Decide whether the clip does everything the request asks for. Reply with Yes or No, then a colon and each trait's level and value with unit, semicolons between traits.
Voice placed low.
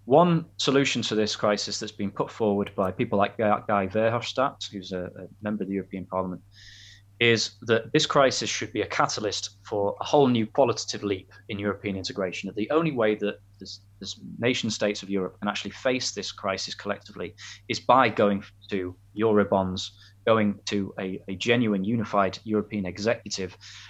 Yes: low, 100 Hz